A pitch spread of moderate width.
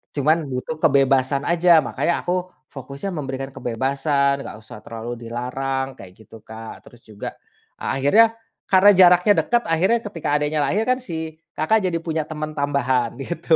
Yes: average, 4.4 semitones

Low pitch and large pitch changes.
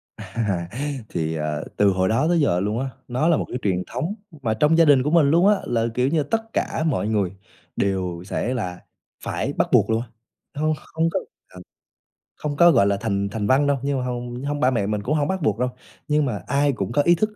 Yes: low, 125 Hz; wide, 6.7 semitones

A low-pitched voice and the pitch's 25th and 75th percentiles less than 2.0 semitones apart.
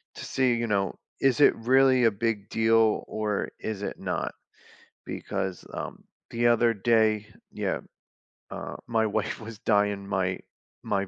No: low, 110 Hz; narrow, 2.4 semitones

